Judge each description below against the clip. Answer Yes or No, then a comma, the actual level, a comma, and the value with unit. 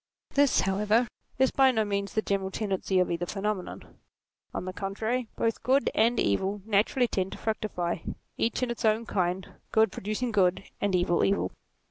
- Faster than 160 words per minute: Yes, average, 170 wpm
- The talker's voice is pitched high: Yes, high, 210 Hz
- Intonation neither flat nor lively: Yes, average, 3.1 semitones